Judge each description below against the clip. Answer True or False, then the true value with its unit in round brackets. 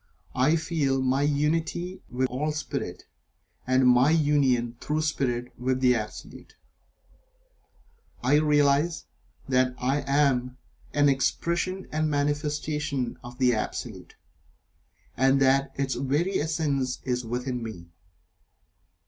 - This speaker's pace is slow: True (110 wpm)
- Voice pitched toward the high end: False (135 Hz)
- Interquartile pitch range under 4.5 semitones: True (2.9 semitones)